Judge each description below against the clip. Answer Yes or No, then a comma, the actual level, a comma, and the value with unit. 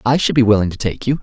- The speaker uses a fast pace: Yes, fast, 345 wpm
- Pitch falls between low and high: No, low, 115 Hz